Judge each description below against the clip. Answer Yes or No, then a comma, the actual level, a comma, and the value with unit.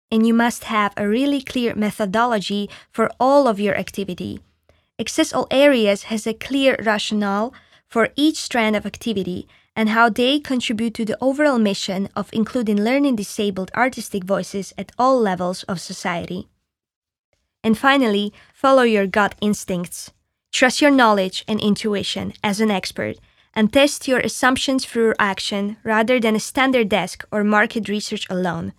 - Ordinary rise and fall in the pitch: Yes, average, 3.4 semitones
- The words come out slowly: No, average, 150 wpm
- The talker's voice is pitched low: No, high, 220 Hz